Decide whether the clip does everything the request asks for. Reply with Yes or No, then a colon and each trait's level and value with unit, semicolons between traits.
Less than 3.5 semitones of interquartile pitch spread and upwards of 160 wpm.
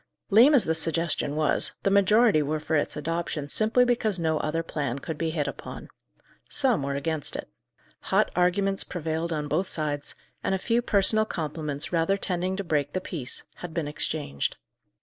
No: average, 4.5 semitones; average, 175 wpm